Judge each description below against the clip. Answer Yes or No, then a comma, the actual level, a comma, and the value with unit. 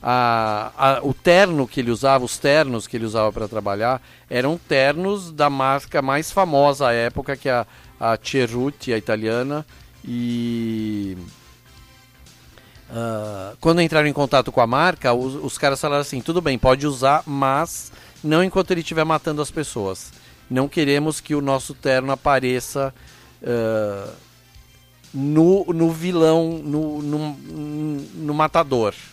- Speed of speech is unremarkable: Yes, average, 145 wpm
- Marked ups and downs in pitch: No, average, 4.2 semitones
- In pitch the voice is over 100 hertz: Yes, low, 135 Hz